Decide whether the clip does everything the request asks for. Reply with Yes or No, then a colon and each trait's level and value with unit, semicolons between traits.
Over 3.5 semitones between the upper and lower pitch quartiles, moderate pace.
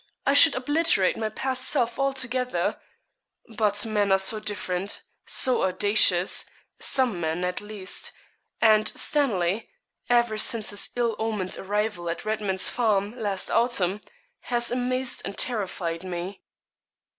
No: average, 4.0 semitones; slow, 125 wpm